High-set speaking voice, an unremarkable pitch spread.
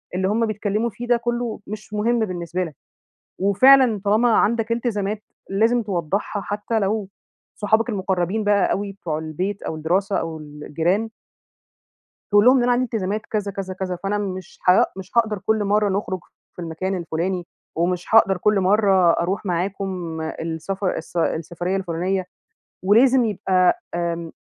Yes: high, 195 Hz; average, 3.2 semitones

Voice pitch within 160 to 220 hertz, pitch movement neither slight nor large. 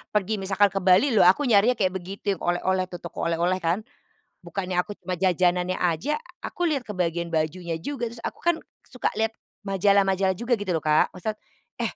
Yes: high, 190 Hz; average, 3.4 semitones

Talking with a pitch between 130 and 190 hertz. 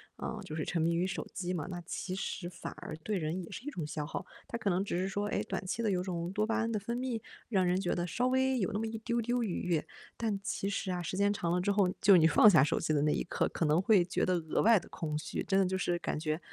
Yes: medium, 185 Hz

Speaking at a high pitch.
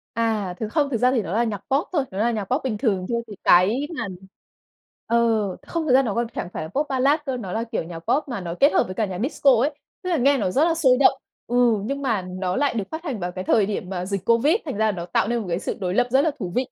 Yes: high, 230 Hz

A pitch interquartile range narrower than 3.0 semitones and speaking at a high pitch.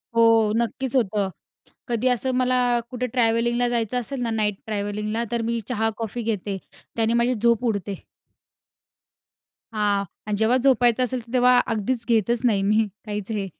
Yes: narrow, 2.6 semitones; high, 230 Hz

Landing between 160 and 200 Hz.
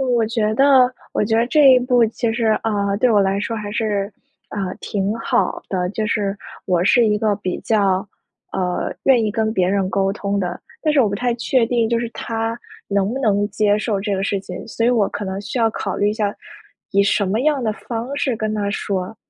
No: high, 215 Hz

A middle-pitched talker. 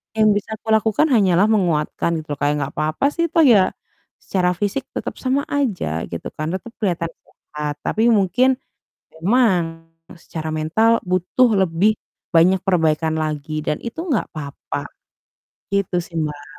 Yes: medium, 180 Hz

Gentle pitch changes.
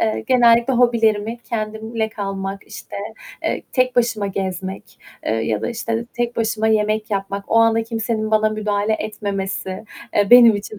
Yes: narrow, 2.2 semitones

